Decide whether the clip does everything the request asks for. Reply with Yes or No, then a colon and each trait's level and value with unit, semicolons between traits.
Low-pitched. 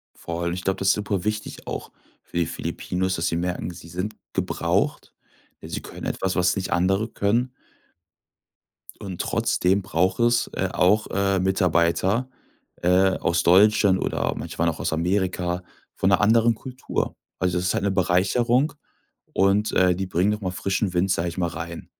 Yes: very low, 95 Hz